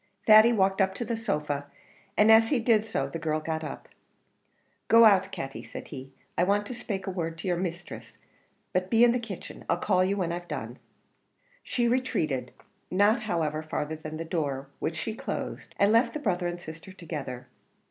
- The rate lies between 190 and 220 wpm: Yes, average, 195 wpm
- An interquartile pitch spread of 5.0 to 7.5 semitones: Yes, wide, 5.4 semitones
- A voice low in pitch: No, medium, 185 Hz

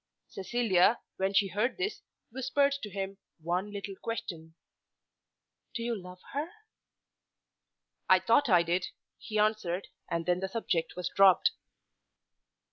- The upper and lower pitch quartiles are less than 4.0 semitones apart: No, average, 4.3 semitones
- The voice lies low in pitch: No, high, 195 Hz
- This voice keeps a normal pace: No, slow, 125 wpm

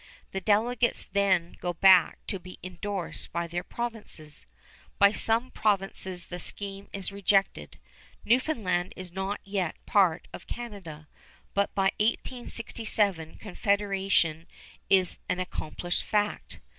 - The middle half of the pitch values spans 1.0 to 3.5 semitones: Yes, average, 2.7 semitones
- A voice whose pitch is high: Yes, high, 195 Hz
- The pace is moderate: No, slow, 120 wpm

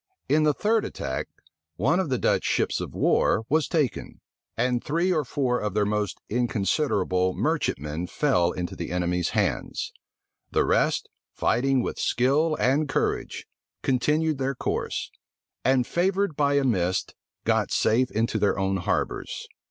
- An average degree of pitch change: No, wide, 7.4 semitones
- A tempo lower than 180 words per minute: Yes, average, 145 wpm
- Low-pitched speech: Yes, low, 125 Hz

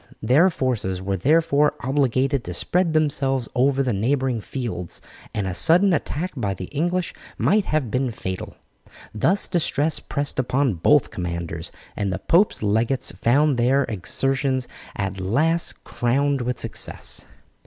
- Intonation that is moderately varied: No, wide, 5.8 semitones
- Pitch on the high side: No, low, 130 Hz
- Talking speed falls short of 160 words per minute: Yes, average, 140 wpm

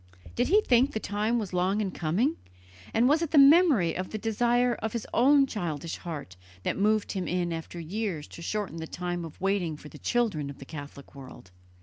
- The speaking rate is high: Yes, fast, 210 wpm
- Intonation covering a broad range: Yes, wide, 6.4 semitones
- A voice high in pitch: Yes, high, 200 Hz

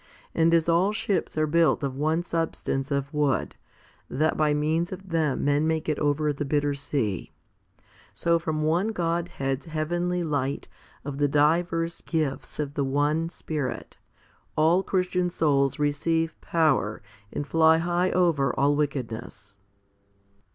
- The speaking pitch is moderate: Yes, medium, 155 Hz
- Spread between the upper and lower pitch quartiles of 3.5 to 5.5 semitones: No, average, 2.8 semitones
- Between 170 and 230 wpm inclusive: No, average, 140 wpm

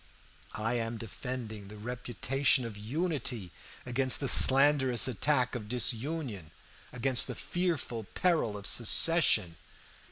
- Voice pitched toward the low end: Yes, low, 125 Hz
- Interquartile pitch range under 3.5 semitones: No, average, 3.8 semitones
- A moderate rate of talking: No, slow, 115 wpm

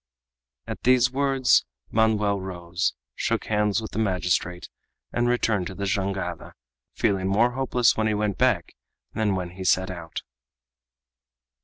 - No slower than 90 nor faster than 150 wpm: Yes, average, 140 wpm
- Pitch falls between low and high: No, low, 100 Hz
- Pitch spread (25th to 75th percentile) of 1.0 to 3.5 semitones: Yes, average, 3.2 semitones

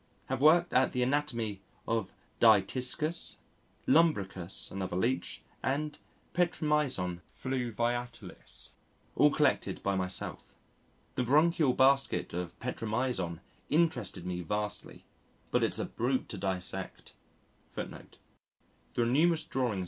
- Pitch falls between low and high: No, low, 120 Hz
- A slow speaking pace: Yes, slow, 100 wpm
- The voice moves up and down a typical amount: No, wide, 6.2 semitones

